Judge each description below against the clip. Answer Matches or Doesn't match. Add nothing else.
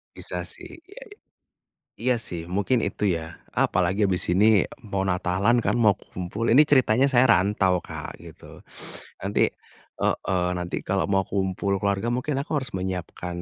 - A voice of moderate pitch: Doesn't match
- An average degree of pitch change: Matches